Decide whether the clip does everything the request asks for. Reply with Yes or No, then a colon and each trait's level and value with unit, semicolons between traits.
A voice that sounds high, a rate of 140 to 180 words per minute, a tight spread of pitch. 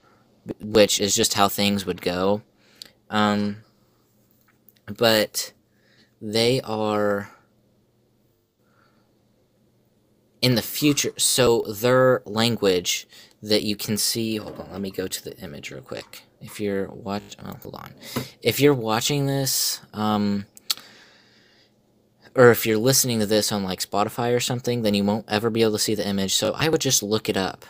No: low, 110 Hz; average, 150 wpm; narrow, 2.0 semitones